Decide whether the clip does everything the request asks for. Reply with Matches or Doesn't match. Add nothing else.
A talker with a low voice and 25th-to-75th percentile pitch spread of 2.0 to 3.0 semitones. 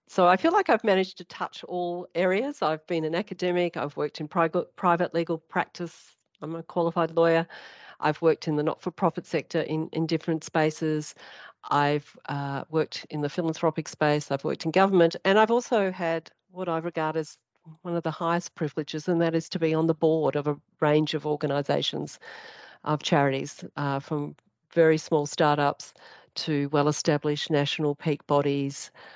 Doesn't match